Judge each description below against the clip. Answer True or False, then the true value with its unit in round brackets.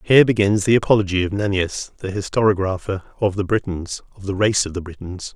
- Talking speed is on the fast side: False (190 wpm)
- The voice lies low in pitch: True (100 Hz)